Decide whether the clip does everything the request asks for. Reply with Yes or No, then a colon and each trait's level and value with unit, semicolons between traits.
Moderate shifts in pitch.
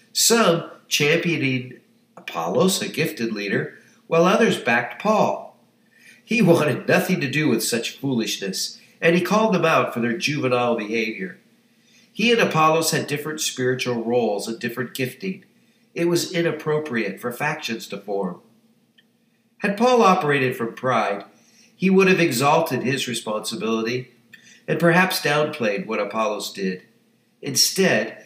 No: wide, 8.2 semitones